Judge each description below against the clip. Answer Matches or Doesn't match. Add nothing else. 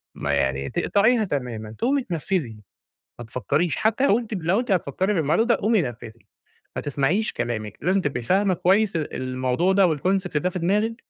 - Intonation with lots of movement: Matches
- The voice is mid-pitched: Matches